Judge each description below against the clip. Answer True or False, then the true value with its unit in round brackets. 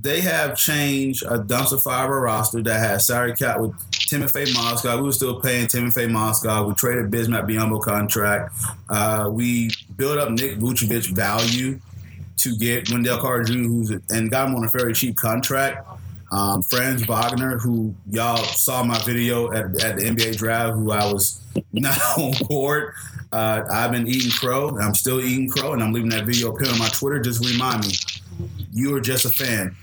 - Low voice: True (115 Hz)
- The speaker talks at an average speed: True (185 wpm)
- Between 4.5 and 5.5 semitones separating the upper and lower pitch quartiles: False (2.7 semitones)